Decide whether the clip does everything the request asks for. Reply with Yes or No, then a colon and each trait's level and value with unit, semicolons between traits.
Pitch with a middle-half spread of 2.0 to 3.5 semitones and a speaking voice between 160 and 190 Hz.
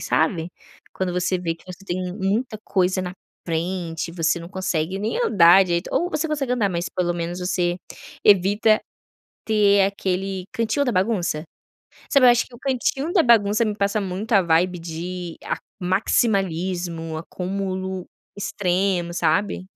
Yes: average, 2.8 semitones; medium, 185 Hz